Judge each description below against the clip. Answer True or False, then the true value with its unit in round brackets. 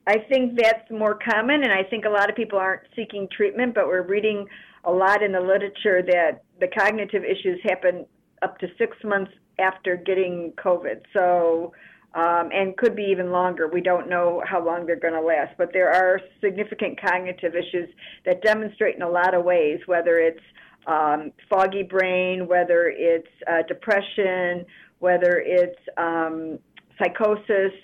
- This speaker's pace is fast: False (165 wpm)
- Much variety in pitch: False (2.7 semitones)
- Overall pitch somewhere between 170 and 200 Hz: True (185 Hz)